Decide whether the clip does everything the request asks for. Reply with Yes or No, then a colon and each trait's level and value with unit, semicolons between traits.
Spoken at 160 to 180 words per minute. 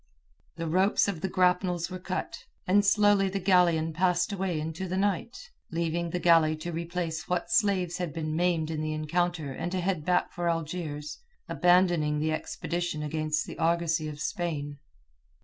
Yes: average, 165 wpm